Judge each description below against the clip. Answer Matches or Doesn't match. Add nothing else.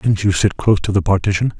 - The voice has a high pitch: Doesn't match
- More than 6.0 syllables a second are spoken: Matches